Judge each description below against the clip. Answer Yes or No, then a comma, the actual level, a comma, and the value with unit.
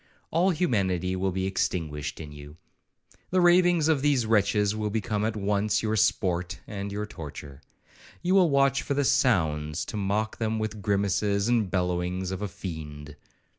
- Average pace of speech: Yes, average, 170 wpm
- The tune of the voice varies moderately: Yes, average, 3.9 semitones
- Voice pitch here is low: Yes, low, 100 Hz